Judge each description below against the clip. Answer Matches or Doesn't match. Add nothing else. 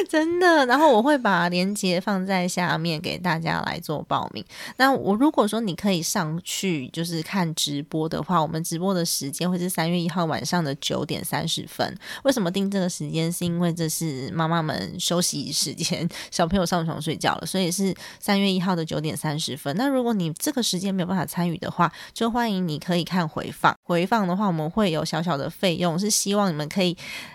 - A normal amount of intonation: Matches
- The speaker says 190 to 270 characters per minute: Doesn't match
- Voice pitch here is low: Doesn't match